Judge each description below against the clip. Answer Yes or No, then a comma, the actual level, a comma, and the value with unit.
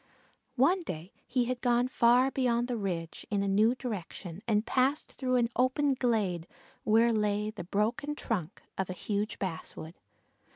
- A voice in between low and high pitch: No, high, 225 Hz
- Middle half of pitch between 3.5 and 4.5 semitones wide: Yes, average, 4.2 semitones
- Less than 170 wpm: Yes, average, 160 wpm